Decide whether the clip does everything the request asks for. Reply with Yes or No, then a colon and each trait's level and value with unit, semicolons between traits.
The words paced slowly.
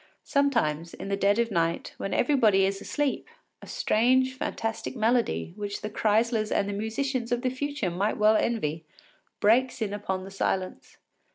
No: average, 165 wpm